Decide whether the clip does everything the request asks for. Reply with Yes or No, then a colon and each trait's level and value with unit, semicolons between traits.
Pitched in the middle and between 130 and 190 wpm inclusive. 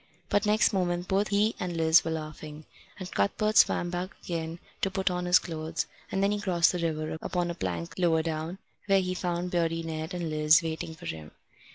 No: medium, 170 Hz; fast, 205 wpm